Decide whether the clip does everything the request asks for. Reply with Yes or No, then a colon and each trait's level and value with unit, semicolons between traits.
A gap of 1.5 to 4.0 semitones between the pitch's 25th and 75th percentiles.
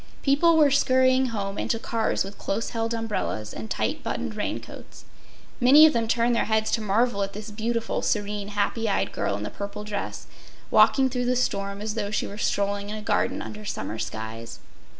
Yes: average, 3.0 semitones